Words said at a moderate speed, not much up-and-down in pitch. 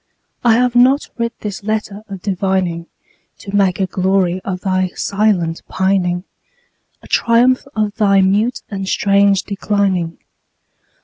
No: slow, 130 wpm; narrow, 2.3 semitones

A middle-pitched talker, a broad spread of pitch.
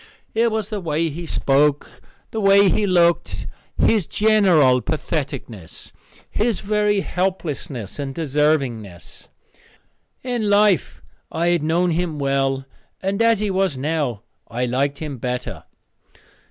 Yes: medium, 160 Hz; wide, 6.4 semitones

